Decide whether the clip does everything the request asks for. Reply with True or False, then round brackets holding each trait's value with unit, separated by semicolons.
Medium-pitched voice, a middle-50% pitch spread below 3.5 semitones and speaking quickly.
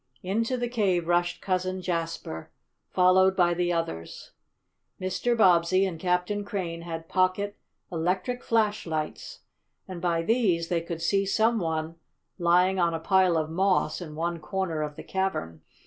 False (180 Hz; 2.4 semitones; 150 wpm)